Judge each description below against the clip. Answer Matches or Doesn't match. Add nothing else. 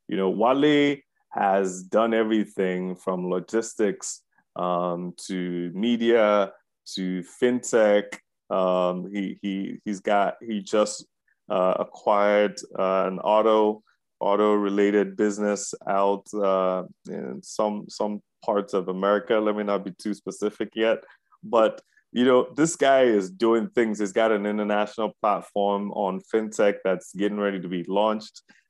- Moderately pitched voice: Doesn't match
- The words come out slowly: Matches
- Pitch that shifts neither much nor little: Doesn't match